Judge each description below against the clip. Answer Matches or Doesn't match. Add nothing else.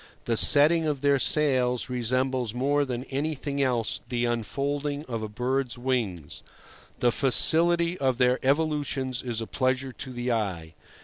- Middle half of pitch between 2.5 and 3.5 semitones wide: Matches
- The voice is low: Matches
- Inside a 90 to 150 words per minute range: Matches